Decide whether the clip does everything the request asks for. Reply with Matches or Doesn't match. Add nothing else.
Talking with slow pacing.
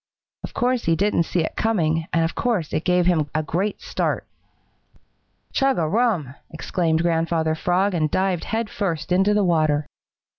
Doesn't match